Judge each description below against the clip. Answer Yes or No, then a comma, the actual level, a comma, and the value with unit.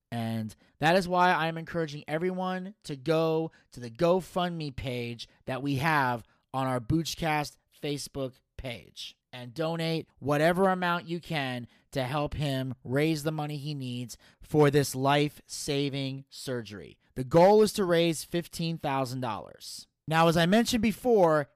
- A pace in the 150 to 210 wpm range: No, average, 140 wpm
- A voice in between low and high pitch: Yes, medium, 150 Hz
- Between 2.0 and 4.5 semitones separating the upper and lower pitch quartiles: Yes, average, 4.2 semitones